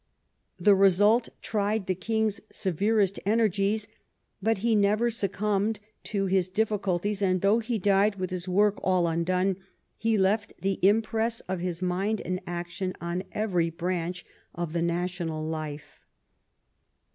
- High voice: Yes, high, 195 Hz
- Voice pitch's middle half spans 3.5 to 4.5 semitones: No, average, 2.9 semitones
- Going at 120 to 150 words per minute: Yes, average, 140 wpm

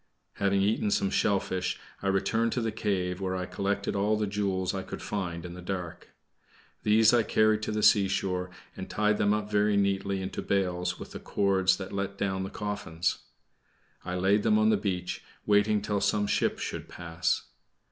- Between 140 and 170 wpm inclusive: No, average, 185 wpm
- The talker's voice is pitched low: Yes, low, 100 Hz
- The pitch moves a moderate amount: No, narrow, 1.9 semitones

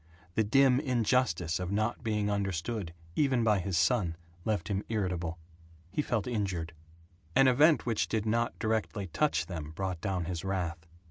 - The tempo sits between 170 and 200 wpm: No, average, 155 wpm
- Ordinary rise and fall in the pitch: Yes, average, 4.7 semitones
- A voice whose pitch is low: Yes, low, 105 Hz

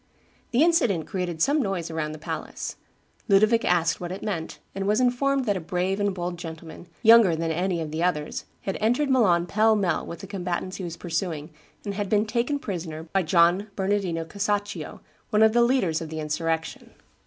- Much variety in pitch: No, average, 4.3 semitones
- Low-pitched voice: No, medium, 185 Hz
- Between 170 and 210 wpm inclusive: Yes, average, 190 wpm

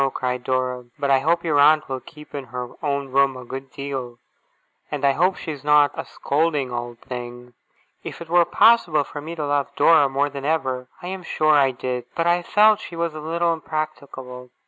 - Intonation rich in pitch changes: No, average, 3.7 semitones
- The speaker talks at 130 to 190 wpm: No, fast, 205 wpm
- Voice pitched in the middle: Yes, medium, 145 Hz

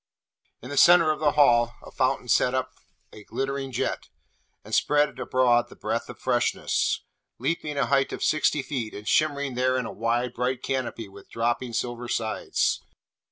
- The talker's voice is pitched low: Yes, low, 130 Hz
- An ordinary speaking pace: Yes, average, 170 wpm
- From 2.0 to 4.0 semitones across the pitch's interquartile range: Yes, average, 2.9 semitones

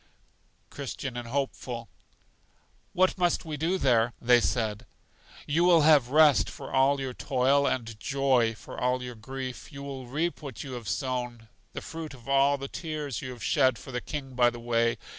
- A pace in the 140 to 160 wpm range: No, average, 180 wpm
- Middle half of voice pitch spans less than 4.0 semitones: Yes, average, 2.8 semitones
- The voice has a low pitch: Yes, low, 130 Hz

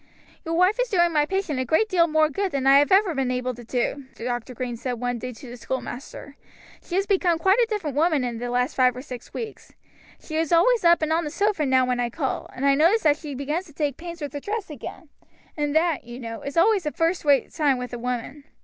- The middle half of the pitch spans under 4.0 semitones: No, average, 5.2 semitones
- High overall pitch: Yes, very high, 295 Hz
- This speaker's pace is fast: Yes, fast, 255 wpm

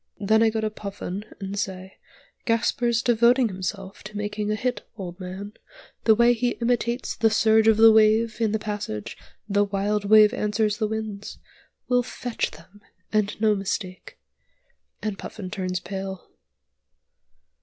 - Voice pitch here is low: No, high, 210 Hz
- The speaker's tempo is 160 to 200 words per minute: No, average, 150 wpm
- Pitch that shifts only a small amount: Yes, narrow, 2.1 semitones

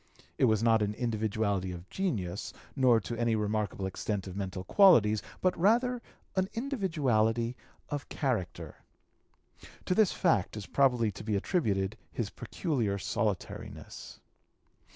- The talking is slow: Yes, slow, 130 wpm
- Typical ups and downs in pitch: No, wide, 6.4 semitones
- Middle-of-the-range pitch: No, low, 110 Hz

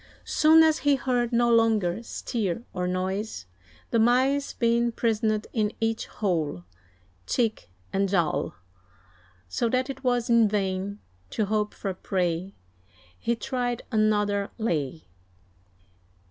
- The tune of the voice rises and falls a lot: No, average, 3.7 semitones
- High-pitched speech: Yes, high, 220 Hz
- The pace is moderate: No, slow, 120 wpm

